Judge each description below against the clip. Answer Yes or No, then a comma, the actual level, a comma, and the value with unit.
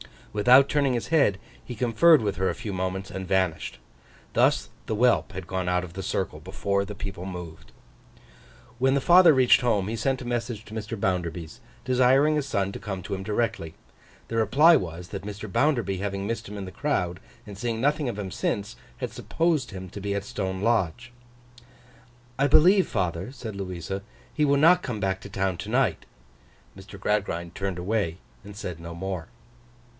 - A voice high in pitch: No, low, 100 Hz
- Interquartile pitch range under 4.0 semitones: No, average, 4.6 semitones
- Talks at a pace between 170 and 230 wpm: Yes, average, 190 wpm